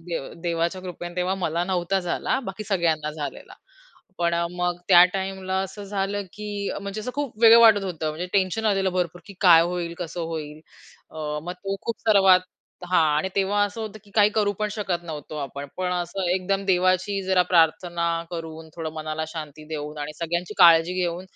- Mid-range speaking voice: Yes, medium, 180 Hz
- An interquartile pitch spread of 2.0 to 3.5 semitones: Yes, average, 2.9 semitones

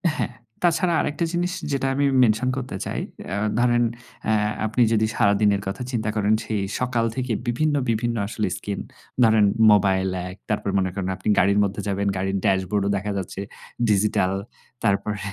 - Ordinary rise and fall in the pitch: Yes, average, 3.5 semitones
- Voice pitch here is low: Yes, low, 105 Hz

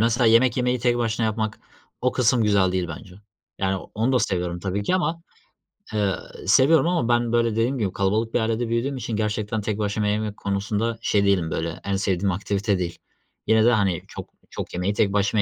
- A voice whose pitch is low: Yes, low, 110 Hz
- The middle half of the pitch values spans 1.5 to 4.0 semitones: Yes, average, 3.0 semitones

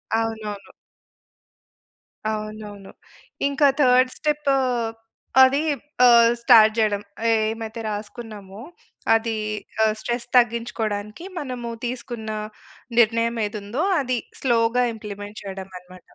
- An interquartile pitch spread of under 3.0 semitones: Yes, narrow, 2.4 semitones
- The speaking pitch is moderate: No, high, 225 Hz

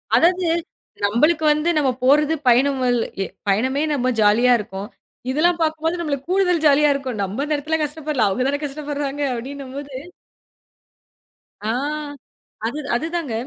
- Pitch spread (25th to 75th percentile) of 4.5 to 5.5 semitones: No, average, 3.4 semitones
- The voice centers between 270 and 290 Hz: Yes, very high, 285 Hz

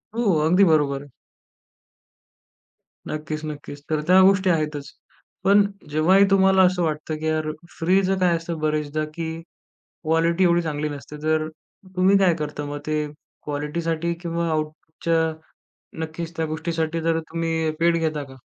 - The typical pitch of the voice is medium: Yes, medium, 160 Hz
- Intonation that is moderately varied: No, narrow, 1.9 semitones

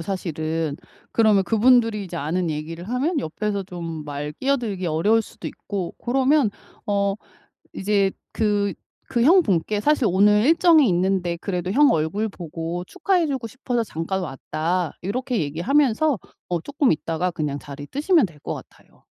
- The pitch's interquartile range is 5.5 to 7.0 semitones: Yes, wide, 6.6 semitones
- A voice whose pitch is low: No, high, 200 Hz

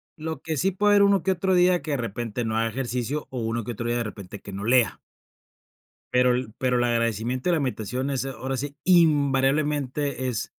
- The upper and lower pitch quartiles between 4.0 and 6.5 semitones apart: Yes, average, 4.3 semitones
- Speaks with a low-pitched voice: Yes, low, 130 Hz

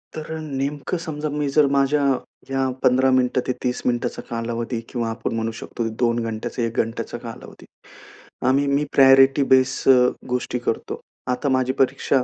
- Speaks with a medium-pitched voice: No, low, 130 Hz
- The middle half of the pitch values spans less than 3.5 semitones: Yes, narrow, 2.6 semitones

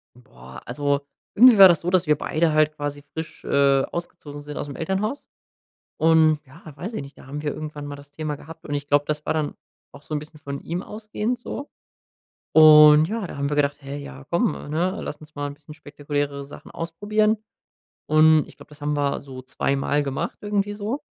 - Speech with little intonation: No, average, 3.0 semitones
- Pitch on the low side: No, medium, 150 Hz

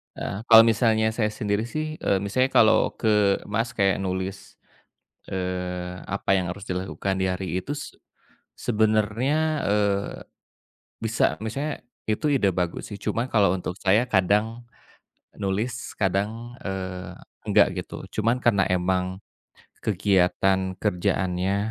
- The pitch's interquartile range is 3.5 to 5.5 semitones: No, average, 2.9 semitones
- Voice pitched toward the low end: Yes, low, 100 Hz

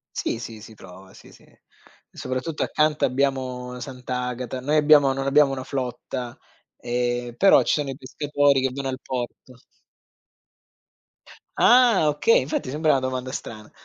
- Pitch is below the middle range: Yes, low, 130 Hz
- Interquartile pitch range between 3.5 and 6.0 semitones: No, narrow, 2.5 semitones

